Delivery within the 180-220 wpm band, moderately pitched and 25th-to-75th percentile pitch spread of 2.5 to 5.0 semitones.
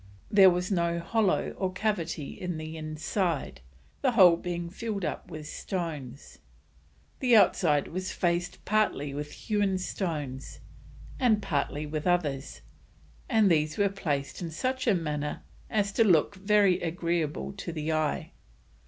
No: average, 140 wpm; medium, 175 Hz; average, 4.3 semitones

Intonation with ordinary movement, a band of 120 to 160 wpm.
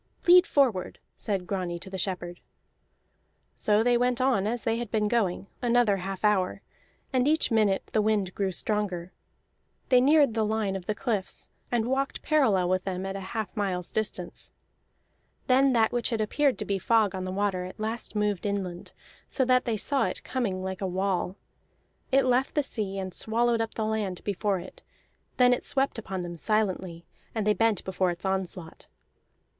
No: average, 4.1 semitones; average, 180 wpm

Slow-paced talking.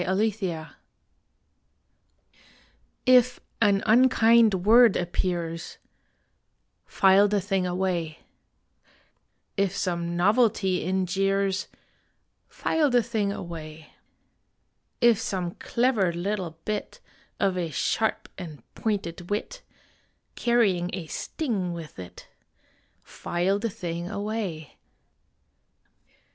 Yes: slow, 90 wpm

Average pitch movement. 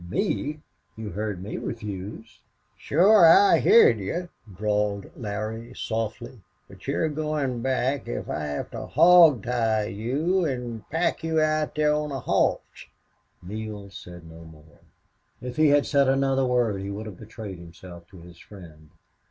No: wide, 6.5 semitones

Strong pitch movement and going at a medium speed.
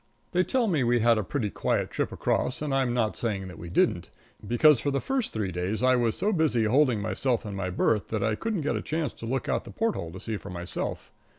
No: wide, 5.7 semitones; fast, 250 wpm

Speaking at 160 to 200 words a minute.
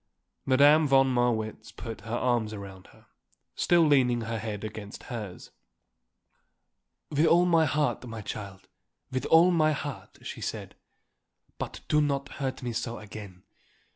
No: average, 140 wpm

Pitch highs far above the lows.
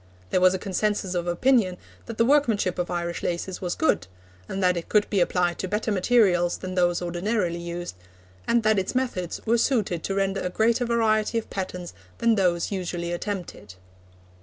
No: average, 3.7 semitones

